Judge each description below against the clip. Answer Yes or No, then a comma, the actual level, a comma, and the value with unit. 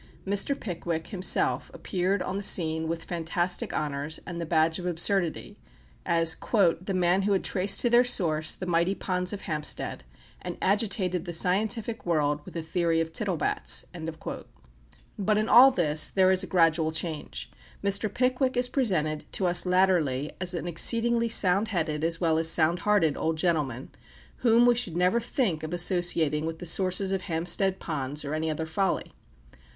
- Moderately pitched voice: Yes, medium, 175 Hz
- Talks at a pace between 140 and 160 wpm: No, average, 170 wpm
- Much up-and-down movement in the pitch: No, average, 3.5 semitones